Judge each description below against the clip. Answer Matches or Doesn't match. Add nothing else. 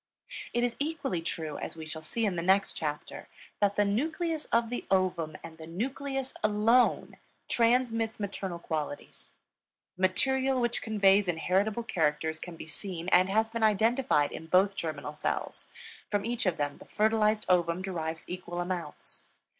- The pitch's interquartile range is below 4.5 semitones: Doesn't match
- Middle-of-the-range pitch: Doesn't match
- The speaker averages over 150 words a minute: Matches